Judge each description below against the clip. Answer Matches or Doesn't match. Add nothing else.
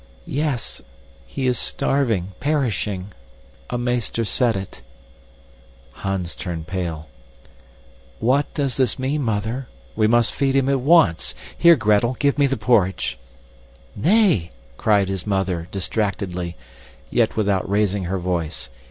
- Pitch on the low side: Matches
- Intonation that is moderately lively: Doesn't match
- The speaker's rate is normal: Doesn't match